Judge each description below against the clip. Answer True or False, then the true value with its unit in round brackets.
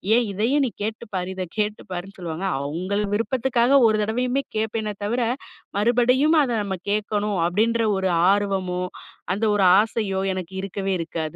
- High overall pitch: True (210 Hz)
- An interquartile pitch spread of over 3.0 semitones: True (3.5 semitones)